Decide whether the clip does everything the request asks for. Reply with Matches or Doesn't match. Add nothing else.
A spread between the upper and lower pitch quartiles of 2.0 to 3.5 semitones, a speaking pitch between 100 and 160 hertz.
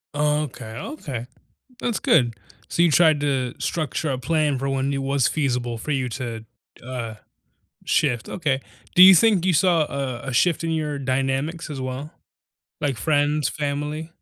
Matches